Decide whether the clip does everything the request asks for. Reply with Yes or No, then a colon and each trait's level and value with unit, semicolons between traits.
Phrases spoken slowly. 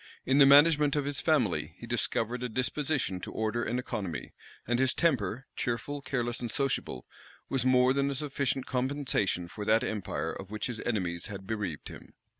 No: average, 180 wpm